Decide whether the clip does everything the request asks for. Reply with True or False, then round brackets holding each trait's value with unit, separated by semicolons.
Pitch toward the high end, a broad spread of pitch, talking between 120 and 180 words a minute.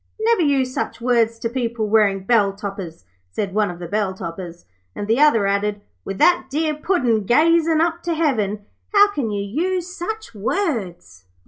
True (230 Hz; 8.0 semitones; 175 wpm)